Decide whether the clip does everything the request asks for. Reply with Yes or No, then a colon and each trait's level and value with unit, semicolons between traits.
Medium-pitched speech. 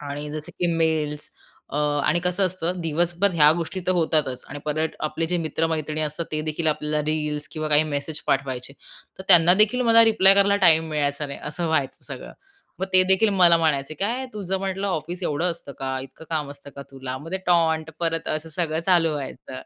Yes: medium, 160 Hz